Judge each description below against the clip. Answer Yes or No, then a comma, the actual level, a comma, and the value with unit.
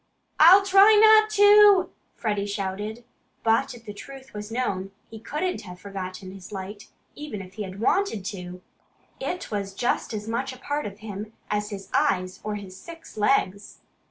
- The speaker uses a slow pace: No, average, 170 wpm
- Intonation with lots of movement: Yes, wide, 6.6 semitones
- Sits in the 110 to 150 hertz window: No, high, 210 Hz